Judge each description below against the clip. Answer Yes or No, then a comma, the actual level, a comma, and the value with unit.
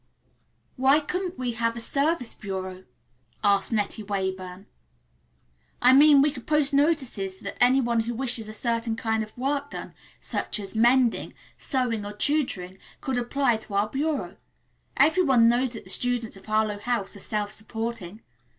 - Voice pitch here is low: No, high, 235 Hz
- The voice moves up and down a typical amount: Yes, average, 4.3 semitones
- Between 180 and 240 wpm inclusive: No, average, 160 wpm